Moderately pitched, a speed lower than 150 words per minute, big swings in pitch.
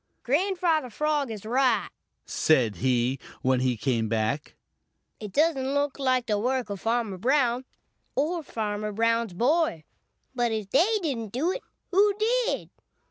No: high, 240 Hz; average, 140 wpm; wide, 6.8 semitones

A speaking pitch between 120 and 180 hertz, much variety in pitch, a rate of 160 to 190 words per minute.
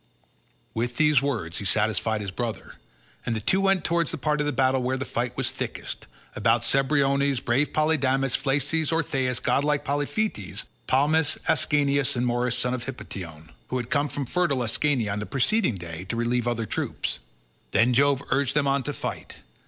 No: low, 135 Hz; average, 3.5 semitones; average, 175 wpm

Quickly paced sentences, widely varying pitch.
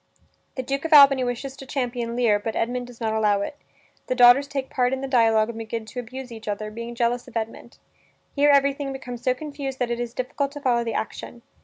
No: fast, 225 wpm; average, 2.7 semitones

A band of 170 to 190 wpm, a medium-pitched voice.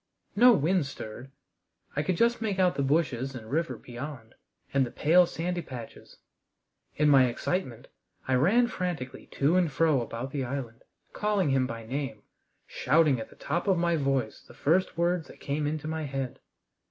Yes: average, 175 wpm; medium, 145 Hz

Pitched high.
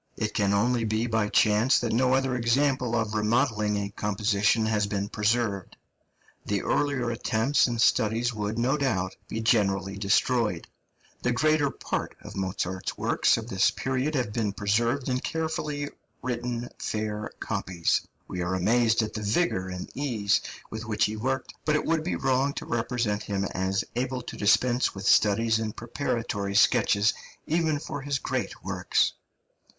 No: low, 115 Hz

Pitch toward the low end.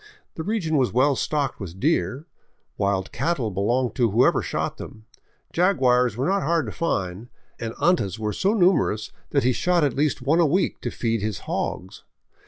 Yes: low, 130 Hz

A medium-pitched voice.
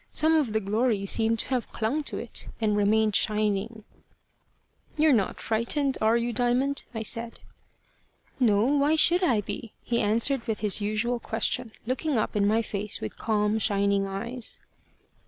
No: high, 225 Hz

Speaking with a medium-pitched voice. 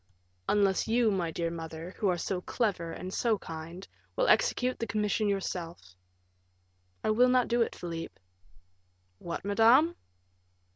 No: high, 200 Hz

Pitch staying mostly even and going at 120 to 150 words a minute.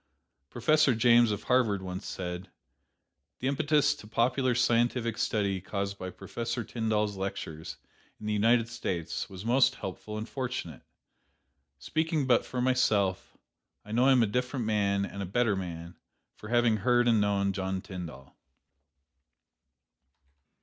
No: average, 3.9 semitones; average, 140 wpm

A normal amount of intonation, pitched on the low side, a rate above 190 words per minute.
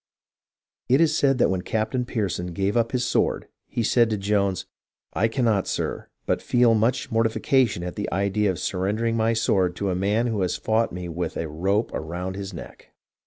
Yes: average, 3.6 semitones; low, 105 Hz; average, 200 wpm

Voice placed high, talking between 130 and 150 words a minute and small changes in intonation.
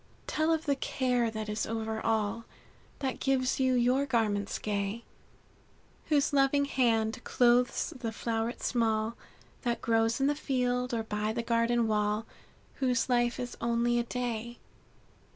Yes: high, 235 Hz; average, 145 wpm; narrow, 2.3 semitones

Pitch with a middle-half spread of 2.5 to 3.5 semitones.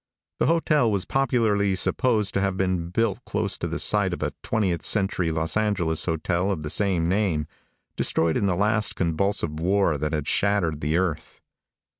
No: average, 4.0 semitones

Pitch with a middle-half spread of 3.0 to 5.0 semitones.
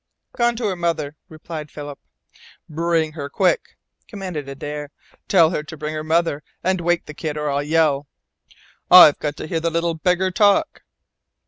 No: narrow, 2.6 semitones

